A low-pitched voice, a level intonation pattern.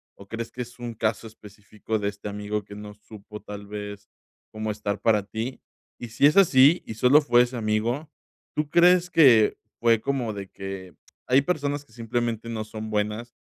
No: low, 110 Hz; average, 3.1 semitones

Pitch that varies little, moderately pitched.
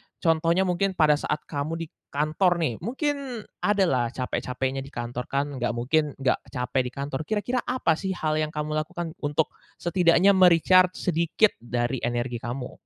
No: wide, 5.4 semitones; medium, 155 Hz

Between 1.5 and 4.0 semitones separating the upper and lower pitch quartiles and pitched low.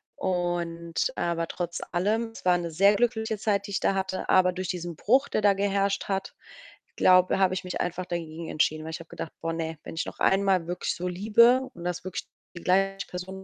No: narrow, 2.4 semitones; medium, 185 Hz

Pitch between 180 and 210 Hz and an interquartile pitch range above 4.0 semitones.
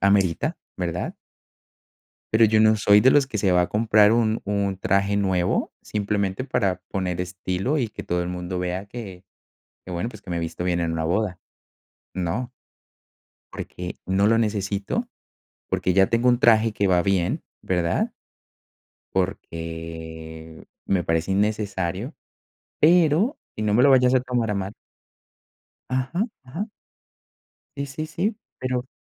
No: low, 100 Hz; average, 4.5 semitones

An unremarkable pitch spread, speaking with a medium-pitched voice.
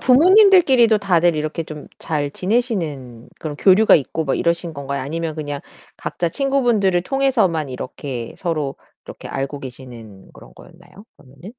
No: wide, 7.0 semitones; medium, 165 Hz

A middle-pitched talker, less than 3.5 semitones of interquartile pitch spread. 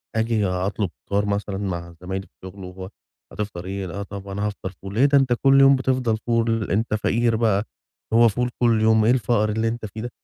No: low, 105 Hz; average, 3.0 semitones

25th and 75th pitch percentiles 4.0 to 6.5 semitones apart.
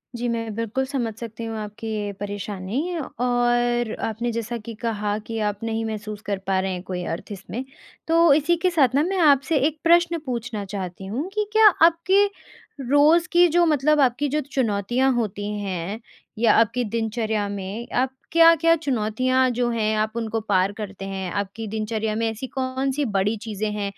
Yes: average, 4.5 semitones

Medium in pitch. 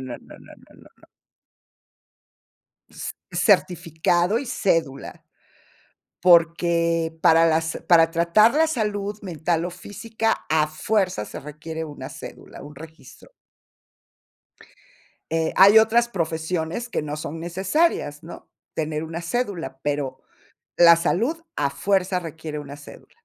Yes: medium, 165 Hz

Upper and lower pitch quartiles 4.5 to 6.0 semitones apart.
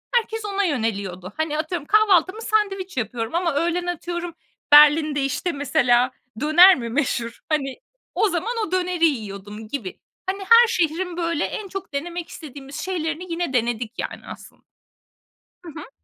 Yes: wide, 5.5 semitones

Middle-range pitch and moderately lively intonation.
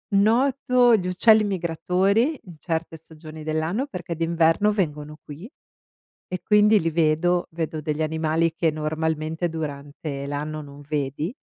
Yes: medium, 165 Hz; average, 3.7 semitones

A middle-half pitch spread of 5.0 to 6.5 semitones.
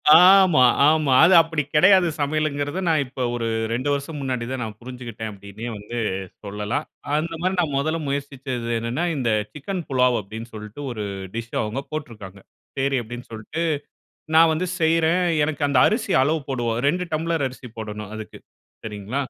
Yes: wide, 5.5 semitones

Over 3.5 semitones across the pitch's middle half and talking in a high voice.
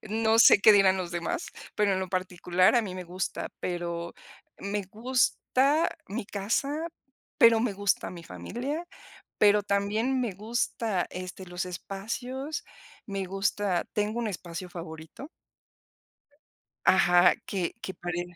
Yes: average, 4.0 semitones; high, 195 Hz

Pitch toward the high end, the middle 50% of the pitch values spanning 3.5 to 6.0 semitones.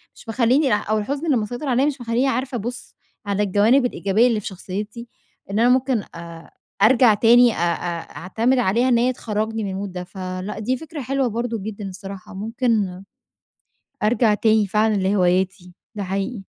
Yes: high, 215 Hz; average, 4.0 semitones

